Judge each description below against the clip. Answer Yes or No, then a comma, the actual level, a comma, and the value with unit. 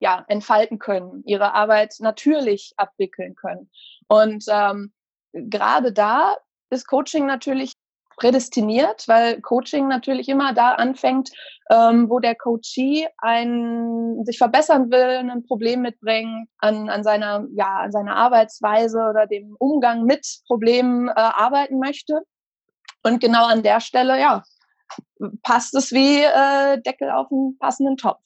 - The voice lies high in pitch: Yes, high, 240 Hz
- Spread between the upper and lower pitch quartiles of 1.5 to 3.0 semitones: No, average, 3.5 semitones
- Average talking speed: Yes, average, 135 wpm